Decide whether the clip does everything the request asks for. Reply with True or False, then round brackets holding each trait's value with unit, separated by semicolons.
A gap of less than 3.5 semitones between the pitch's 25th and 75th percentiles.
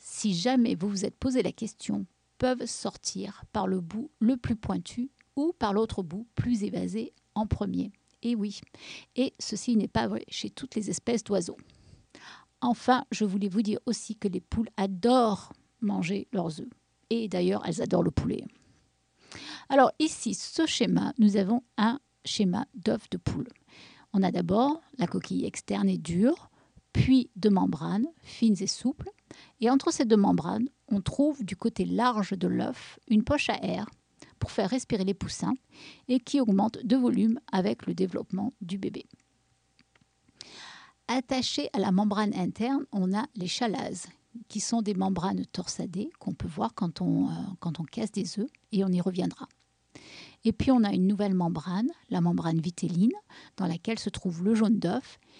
False (4.0 semitones)